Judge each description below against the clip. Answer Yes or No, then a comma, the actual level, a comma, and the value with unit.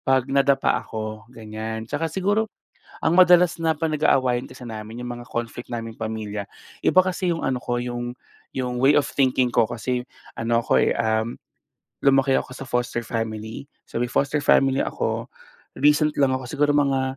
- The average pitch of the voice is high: No, low, 125 Hz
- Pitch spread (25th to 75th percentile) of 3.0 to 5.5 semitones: Yes, average, 3.8 semitones